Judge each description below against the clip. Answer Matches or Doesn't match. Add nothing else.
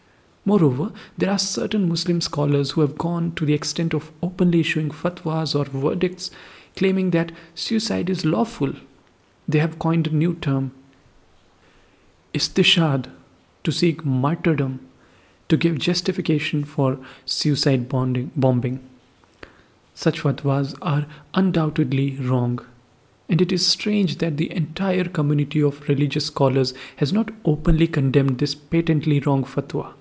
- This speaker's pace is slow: Matches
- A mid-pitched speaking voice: Matches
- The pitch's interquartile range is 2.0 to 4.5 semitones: Matches